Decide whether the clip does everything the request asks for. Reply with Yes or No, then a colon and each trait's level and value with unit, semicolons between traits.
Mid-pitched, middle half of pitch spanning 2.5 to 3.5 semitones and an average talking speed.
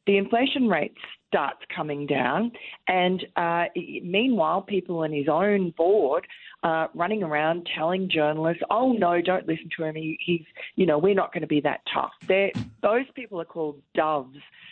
No: medium, 175 Hz; average, 4.2 semitones; average, 175 wpm